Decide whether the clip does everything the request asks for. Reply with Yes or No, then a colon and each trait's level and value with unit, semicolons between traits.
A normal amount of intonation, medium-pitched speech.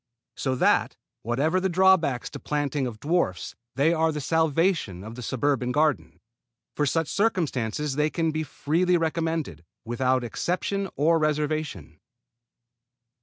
Yes: average, 4.2 semitones; medium, 150 Hz